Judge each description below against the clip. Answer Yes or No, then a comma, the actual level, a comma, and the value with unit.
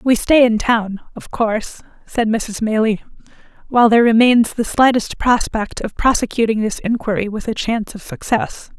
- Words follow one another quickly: No, average, 165 wpm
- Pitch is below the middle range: No, high, 225 Hz